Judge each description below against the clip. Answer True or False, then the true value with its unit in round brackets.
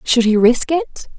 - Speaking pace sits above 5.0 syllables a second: True (5.3 syllables/s)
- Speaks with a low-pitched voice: False (260 Hz)